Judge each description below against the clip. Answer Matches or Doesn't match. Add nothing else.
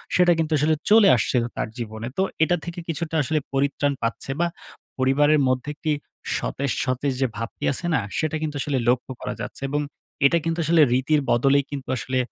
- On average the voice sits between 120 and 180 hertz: Matches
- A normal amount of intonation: Matches